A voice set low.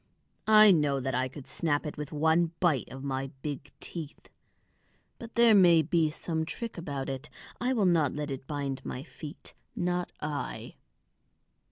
No: medium, 150 Hz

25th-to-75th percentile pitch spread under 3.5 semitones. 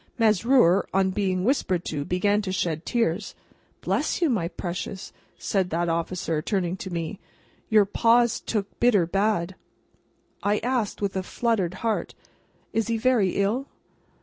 No: average, 3.9 semitones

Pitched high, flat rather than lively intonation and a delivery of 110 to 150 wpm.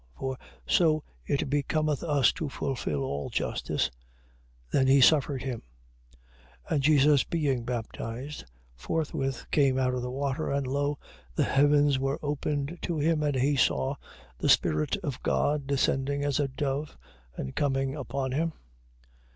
No: medium, 140 Hz; narrow, 2.0 semitones; average, 145 wpm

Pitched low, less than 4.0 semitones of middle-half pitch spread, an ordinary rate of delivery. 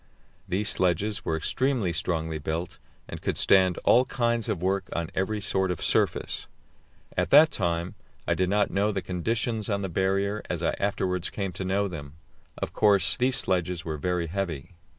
Yes: very low, 95 Hz; average, 3.0 semitones; average, 175 wpm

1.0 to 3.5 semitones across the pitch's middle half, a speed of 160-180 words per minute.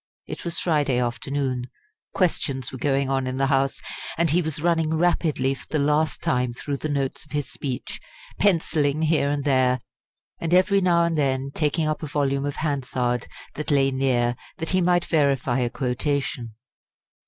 Yes: average, 3.2 semitones; average, 175 wpm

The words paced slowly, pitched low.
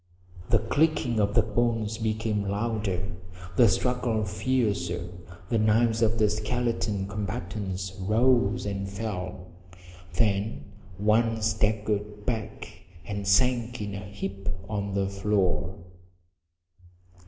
Yes: slow, 110 wpm; low, 105 Hz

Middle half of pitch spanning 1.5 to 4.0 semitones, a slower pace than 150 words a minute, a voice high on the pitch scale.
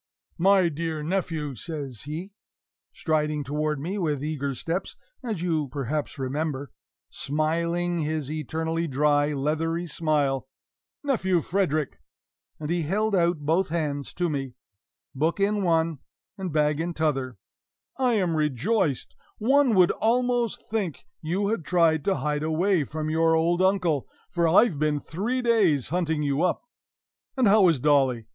No: average, 3.6 semitones; average, 140 wpm; medium, 160 Hz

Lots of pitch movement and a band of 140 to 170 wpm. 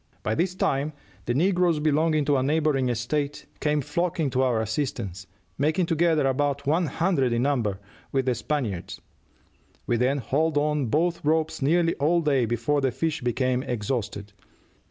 No: average, 4.0 semitones; average, 155 wpm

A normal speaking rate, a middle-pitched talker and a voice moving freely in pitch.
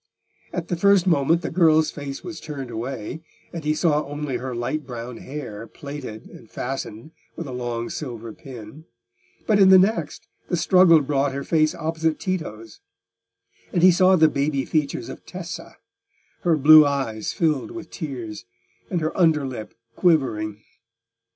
No: average, 155 wpm; medium, 150 Hz; average, 4.8 semitones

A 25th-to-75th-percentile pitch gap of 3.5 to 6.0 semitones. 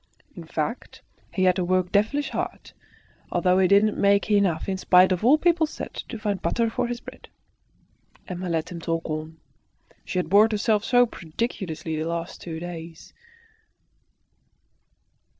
Yes: average, 4.2 semitones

